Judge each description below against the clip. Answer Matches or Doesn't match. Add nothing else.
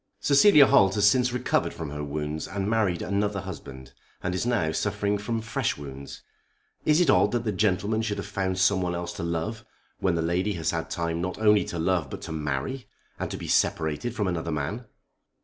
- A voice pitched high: Doesn't match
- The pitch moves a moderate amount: Matches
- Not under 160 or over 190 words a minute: Doesn't match